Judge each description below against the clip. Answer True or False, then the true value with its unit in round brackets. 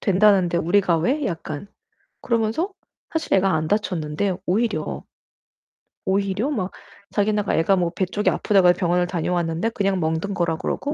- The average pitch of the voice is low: False (190 Hz)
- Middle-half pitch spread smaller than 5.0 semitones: True (3.3 semitones)